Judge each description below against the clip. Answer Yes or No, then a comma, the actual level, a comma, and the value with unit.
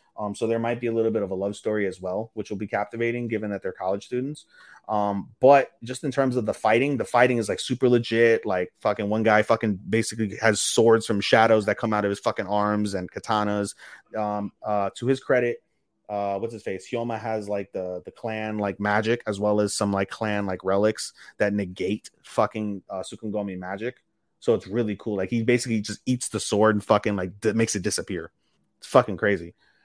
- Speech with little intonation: Yes, narrow, 2.1 semitones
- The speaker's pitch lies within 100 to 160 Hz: Yes, low, 105 Hz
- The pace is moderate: No, fast, 215 wpm